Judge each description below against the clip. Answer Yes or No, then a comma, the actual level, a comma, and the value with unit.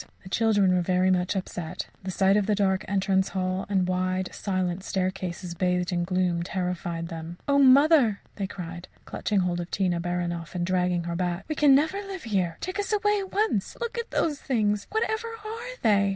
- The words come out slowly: No, average, 195 wpm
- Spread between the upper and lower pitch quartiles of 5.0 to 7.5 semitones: No, average, 4.4 semitones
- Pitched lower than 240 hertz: Yes, high, 190 Hz